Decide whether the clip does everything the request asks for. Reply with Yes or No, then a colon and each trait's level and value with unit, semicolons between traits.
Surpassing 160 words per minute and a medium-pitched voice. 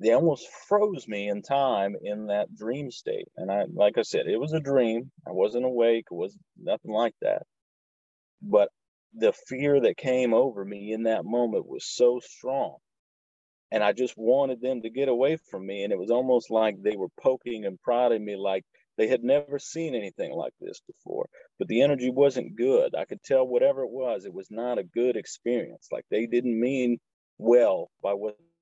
No: average, 195 wpm; low, 125 Hz